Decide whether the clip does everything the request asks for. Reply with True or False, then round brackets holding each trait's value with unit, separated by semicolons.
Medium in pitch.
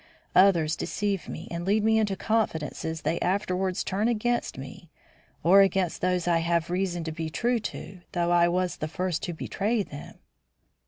True (180 Hz)